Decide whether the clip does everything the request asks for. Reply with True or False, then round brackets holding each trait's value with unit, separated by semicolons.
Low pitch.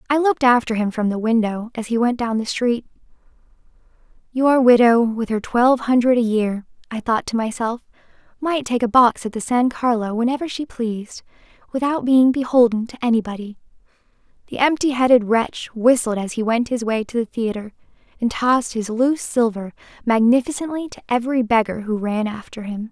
False (235 Hz)